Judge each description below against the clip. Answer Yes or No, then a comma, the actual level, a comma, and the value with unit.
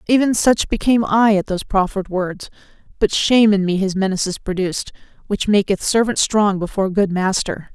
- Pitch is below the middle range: No, high, 200 Hz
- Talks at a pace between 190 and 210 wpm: No, average, 170 wpm